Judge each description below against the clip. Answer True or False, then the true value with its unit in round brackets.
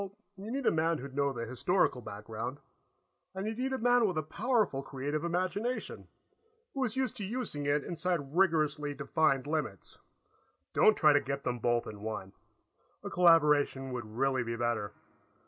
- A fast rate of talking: False (170 wpm)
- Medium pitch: True (150 Hz)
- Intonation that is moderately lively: False (6.7 semitones)